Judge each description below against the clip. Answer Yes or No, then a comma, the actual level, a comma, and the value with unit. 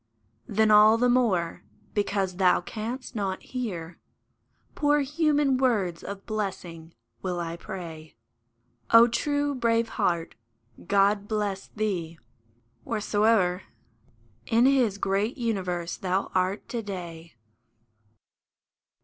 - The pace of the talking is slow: Yes, slow, 105 wpm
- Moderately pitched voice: No, high, 205 Hz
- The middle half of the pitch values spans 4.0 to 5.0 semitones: Yes, average, 4.3 semitones